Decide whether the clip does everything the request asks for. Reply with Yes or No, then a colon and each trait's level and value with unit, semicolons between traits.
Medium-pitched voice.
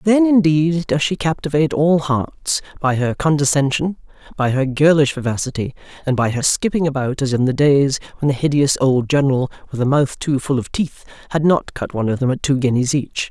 Yes: medium, 145 Hz